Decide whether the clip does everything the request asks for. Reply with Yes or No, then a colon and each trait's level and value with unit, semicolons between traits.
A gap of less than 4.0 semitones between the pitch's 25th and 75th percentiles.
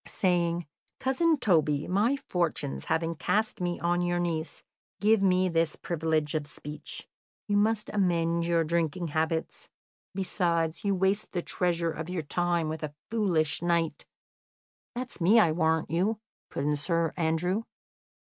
Yes: average, 2.9 semitones